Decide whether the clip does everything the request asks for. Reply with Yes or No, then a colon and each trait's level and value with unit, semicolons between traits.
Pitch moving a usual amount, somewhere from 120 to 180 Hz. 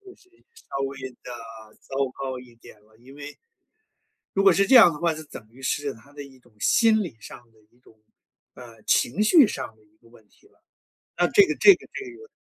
No: wide, 8.9 semitones; medium, 140 Hz